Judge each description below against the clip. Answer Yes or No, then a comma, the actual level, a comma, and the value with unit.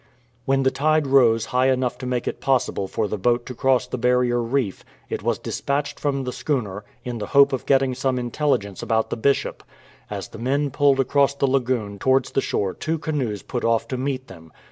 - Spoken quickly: Yes, fast, 210 wpm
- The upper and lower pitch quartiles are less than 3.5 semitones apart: Yes, average, 2.8 semitones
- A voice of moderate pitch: No, low, 130 Hz